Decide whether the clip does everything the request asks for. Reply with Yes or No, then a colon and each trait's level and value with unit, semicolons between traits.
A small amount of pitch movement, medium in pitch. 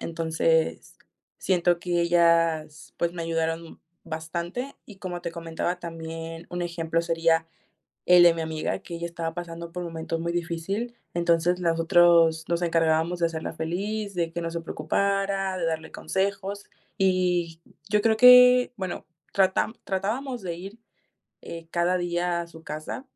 Yes: narrow, 2.0 semitones; medium, 170 Hz